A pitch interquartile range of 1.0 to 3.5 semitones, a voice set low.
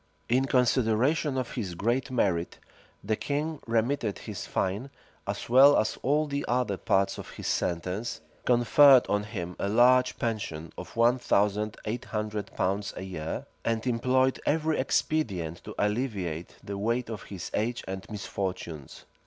No: average, 4.5 semitones; low, 110 Hz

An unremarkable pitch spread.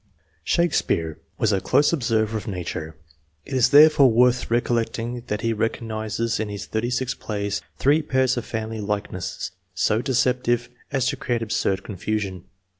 Yes: average, 3.0 semitones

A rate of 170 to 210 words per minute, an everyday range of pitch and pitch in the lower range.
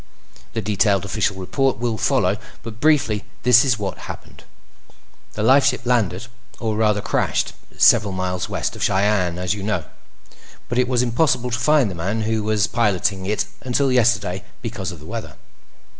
No: average, 160 wpm; average, 3.6 semitones; low, 110 Hz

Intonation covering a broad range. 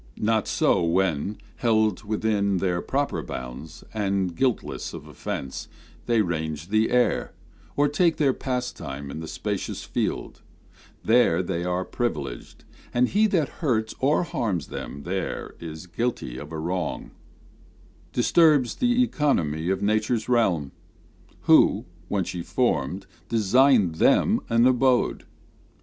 Yes: wide, 6.7 semitones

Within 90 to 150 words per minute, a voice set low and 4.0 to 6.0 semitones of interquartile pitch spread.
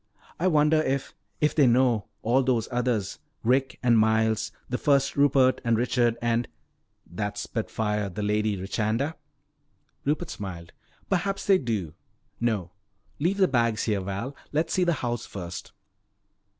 Yes: average, 145 wpm; low, 120 Hz; average, 4.7 semitones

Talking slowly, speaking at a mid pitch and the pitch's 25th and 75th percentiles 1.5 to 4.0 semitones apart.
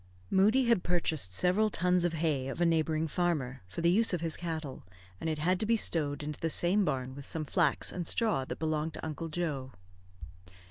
No: fast, 205 wpm; medium, 165 Hz; average, 3.0 semitones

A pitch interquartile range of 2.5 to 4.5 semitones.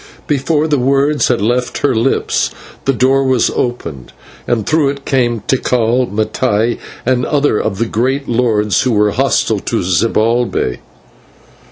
Yes: average, 3.5 semitones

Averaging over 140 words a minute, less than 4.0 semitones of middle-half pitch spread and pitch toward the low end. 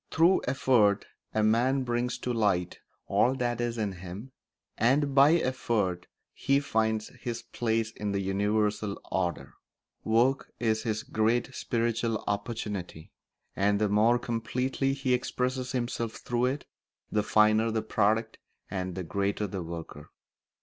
No: slow, 135 wpm; average, 3.3 semitones; low, 110 Hz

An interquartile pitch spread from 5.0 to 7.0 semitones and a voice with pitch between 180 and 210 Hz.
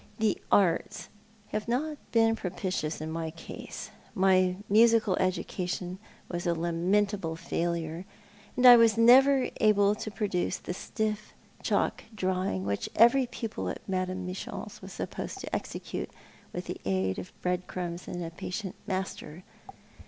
No: average, 3.8 semitones; medium, 185 Hz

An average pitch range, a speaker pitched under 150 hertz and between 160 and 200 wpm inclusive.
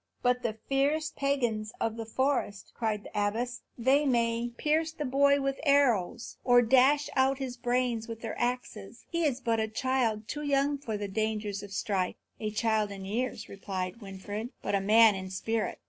No: average, 4.0 semitones; high, 230 Hz; average, 185 wpm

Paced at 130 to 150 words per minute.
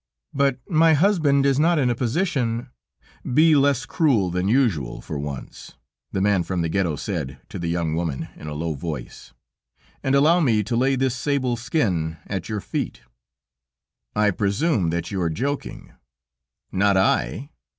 No: average, 165 wpm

